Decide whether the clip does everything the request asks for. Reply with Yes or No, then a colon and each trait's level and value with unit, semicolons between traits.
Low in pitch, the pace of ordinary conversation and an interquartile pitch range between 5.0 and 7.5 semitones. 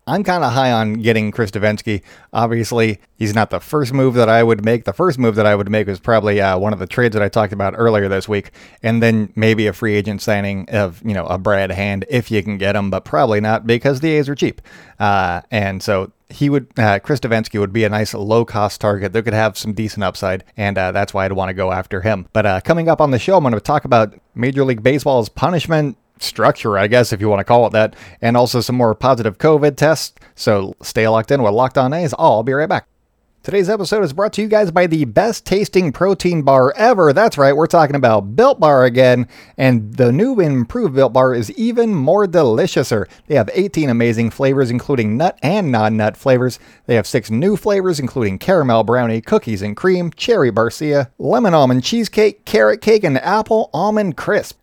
No: low, 115 Hz; fast, 225 wpm; average, 5.3 semitones